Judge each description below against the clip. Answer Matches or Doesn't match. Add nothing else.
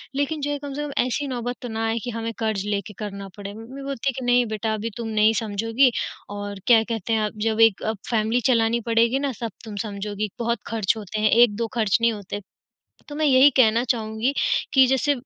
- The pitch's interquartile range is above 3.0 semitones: Doesn't match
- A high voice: Matches